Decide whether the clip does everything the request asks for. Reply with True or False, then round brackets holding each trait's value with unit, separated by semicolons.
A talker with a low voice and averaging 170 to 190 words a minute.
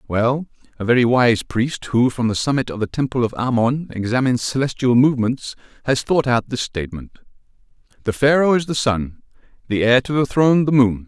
True (125 Hz; 185 wpm)